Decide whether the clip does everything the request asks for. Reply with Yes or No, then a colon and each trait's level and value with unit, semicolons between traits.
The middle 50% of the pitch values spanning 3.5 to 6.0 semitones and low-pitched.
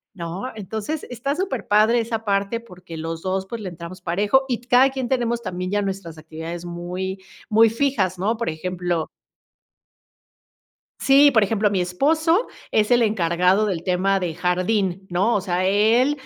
No: average, 4.6 semitones; high, 195 Hz